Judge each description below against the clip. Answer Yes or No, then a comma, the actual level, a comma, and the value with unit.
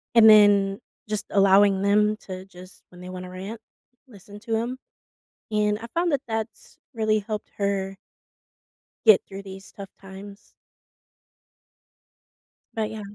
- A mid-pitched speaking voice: No, high, 205 Hz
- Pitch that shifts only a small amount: Yes, narrow, 2.0 semitones